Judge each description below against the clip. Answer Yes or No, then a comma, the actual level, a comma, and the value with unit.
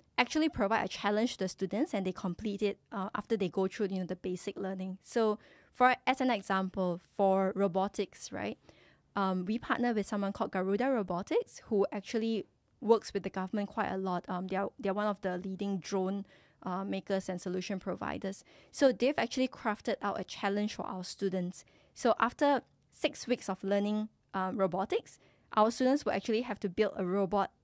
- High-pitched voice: Yes, high, 200 Hz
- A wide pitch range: No, average, 2.7 semitones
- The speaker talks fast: No, average, 190 wpm